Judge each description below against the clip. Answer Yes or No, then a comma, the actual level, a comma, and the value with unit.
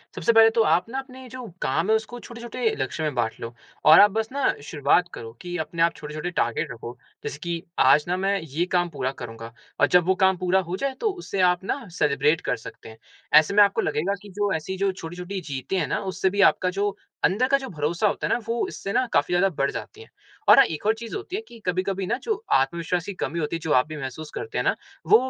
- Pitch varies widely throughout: Yes, wide, 6.3 semitones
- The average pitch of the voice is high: No, medium, 180 Hz